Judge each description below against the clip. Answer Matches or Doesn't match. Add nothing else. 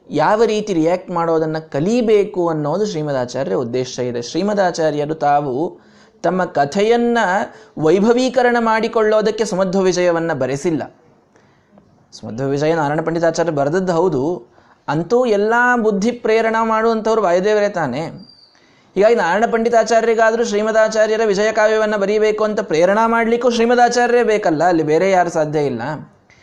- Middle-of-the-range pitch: Doesn't match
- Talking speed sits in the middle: Doesn't match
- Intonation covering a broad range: Matches